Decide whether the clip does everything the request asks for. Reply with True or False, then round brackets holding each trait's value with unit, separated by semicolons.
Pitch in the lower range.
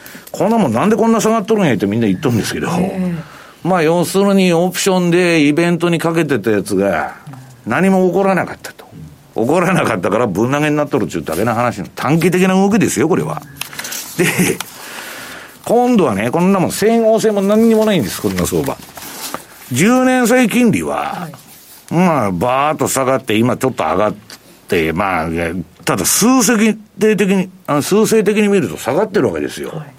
False (180 Hz)